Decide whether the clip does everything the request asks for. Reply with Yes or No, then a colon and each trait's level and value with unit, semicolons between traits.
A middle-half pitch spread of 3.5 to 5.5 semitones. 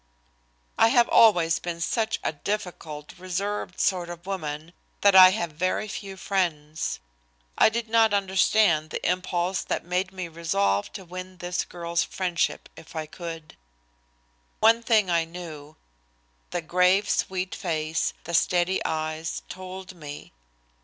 No: average, 2.8 semitones